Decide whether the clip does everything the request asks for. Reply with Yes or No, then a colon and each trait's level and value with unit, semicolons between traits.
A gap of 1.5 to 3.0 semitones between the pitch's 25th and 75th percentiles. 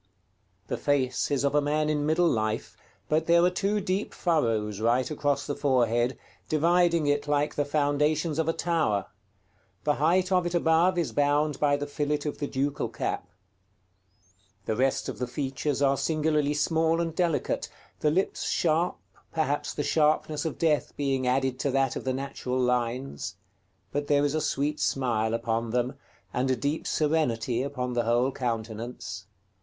No: average, 3.6 semitones